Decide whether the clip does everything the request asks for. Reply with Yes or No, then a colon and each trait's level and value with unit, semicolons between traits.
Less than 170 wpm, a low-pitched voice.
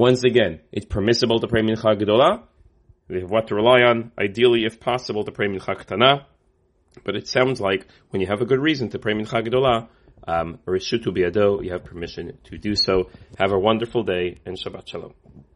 No: average, 200 wpm; low, 110 Hz